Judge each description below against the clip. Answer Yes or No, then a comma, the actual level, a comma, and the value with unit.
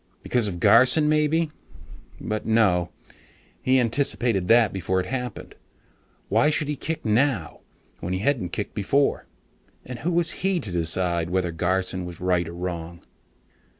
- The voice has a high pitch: No, low, 105 Hz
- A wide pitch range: Yes, wide, 7.4 semitones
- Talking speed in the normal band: Yes, average, 150 wpm